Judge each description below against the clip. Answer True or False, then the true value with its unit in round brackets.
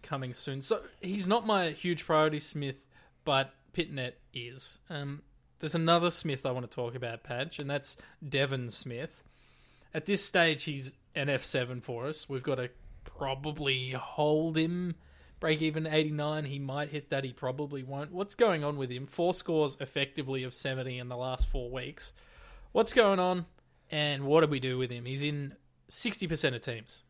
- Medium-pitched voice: True (145 Hz)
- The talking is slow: False (175 wpm)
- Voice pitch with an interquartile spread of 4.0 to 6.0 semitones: False (3.5 semitones)